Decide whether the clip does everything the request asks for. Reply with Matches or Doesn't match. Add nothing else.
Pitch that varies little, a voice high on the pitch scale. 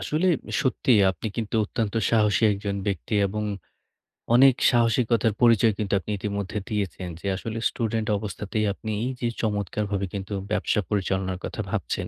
Doesn't match